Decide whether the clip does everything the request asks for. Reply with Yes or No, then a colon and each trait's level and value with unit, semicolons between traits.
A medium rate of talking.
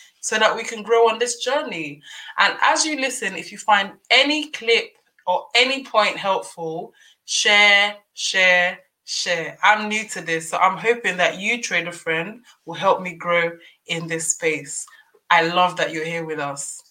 Yes: average, 175 wpm